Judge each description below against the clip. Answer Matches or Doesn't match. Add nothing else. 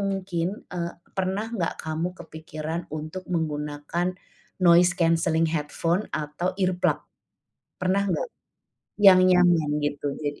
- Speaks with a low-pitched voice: Doesn't match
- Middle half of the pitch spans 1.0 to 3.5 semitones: Matches